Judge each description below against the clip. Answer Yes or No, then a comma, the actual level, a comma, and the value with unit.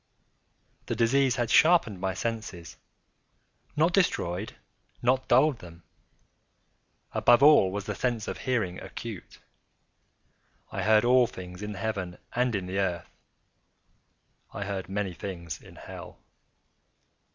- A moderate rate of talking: No, slow, 120 wpm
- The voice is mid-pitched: No, low, 105 Hz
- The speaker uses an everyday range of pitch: Yes, average, 5.0 semitones